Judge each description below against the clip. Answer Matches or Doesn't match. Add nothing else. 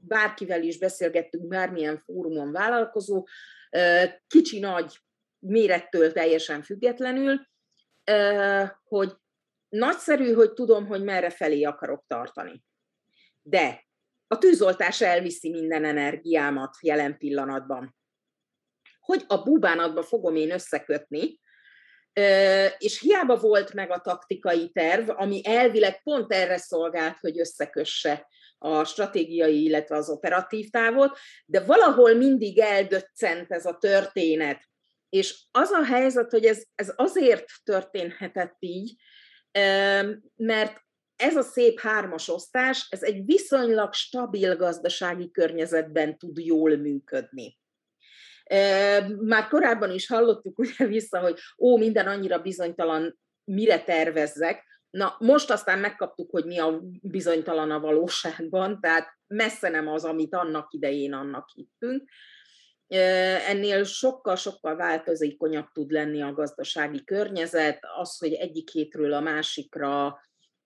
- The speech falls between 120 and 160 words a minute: Doesn't match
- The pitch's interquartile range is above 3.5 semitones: Matches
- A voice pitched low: Doesn't match